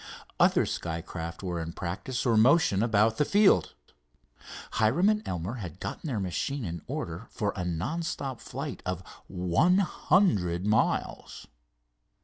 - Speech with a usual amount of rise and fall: No, wide, 7.5 semitones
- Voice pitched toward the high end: No, low, 105 Hz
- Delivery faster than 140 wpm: No, slow, 135 wpm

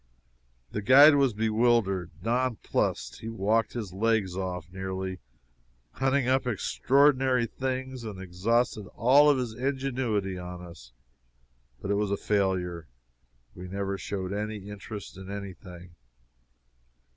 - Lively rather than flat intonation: No, average, 4.7 semitones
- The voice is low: Yes, low, 105 Hz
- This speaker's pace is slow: Yes, slow, 125 wpm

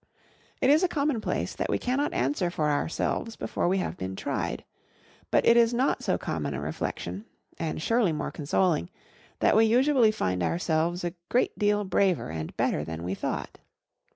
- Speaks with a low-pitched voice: No, medium, 185 Hz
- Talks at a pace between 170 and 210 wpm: Yes, average, 175 wpm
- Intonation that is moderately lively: No, wide, 7.7 semitones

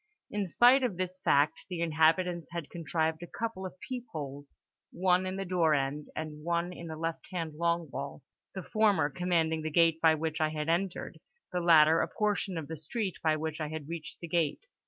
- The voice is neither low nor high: Yes, medium, 165 Hz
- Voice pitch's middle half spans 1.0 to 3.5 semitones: Yes, narrow, 2.6 semitones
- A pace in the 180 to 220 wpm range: Yes, average, 200 wpm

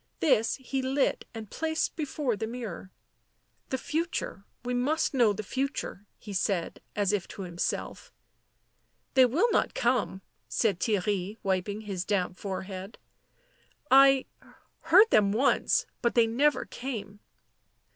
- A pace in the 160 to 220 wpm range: No, average, 150 wpm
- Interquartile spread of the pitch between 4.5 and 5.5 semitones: Yes, average, 5.2 semitones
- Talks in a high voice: Yes, high, 225 Hz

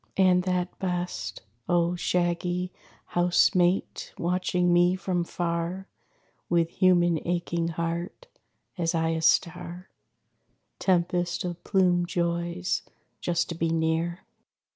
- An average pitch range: No, narrow, 1.0 semitones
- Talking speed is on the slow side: Yes, slow, 110 wpm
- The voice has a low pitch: No, medium, 175 Hz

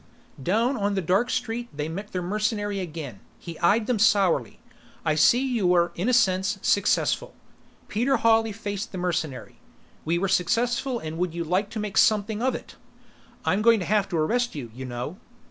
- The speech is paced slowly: No, average, 185 wpm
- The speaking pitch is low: No, high, 200 Hz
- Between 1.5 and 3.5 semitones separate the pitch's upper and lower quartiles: No, average, 4.7 semitones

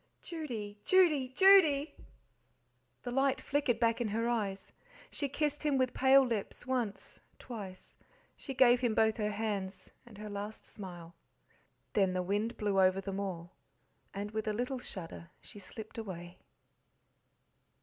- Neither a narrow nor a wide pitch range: Yes, average, 4.6 semitones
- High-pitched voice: Yes, high, 220 Hz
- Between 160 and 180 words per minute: No, average, 145 wpm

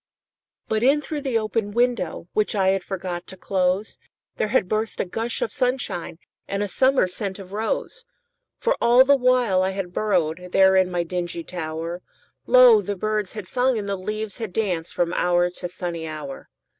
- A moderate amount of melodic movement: Yes, average, 4.7 semitones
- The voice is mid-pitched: No, high, 195 Hz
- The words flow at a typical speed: Yes, average, 160 wpm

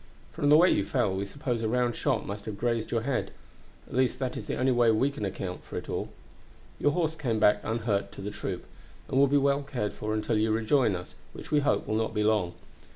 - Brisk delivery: Yes, fast, 240 wpm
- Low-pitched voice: Yes, low, 115 Hz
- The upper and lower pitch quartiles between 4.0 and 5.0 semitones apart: Yes, average, 4.3 semitones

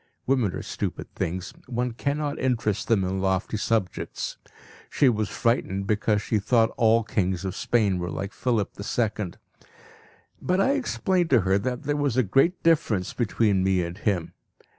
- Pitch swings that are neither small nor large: Yes, average, 4.8 semitones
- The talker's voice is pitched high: No, low, 110 Hz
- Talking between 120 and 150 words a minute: No, average, 160 wpm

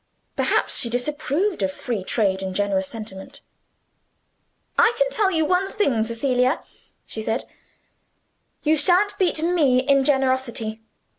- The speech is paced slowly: Yes, slow, 130 wpm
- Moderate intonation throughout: No, wide, 6.6 semitones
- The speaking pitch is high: Yes, very high, 265 Hz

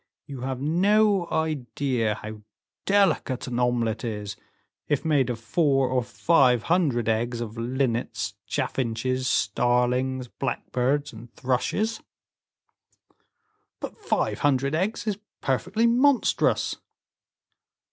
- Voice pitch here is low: Yes, low, 130 Hz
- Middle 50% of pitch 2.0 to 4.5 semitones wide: No, average, 4.9 semitones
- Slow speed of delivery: Yes, slow, 105 wpm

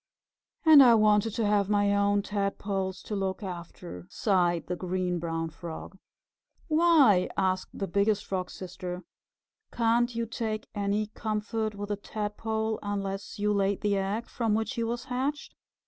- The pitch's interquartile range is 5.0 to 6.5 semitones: No, average, 2.7 semitones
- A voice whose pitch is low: No, high, 205 Hz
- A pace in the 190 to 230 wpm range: No, average, 150 wpm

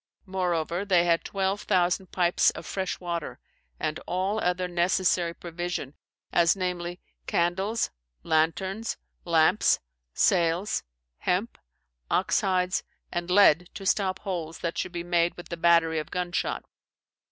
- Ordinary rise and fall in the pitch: No, narrow, 1.6 semitones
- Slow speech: Yes, slow, 130 wpm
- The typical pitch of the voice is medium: Yes, medium, 175 Hz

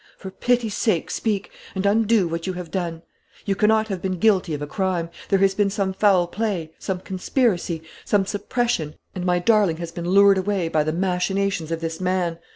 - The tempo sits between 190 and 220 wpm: Yes, average, 195 wpm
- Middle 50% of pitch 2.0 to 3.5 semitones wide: Yes, average, 2.9 semitones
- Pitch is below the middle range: No, high, 190 Hz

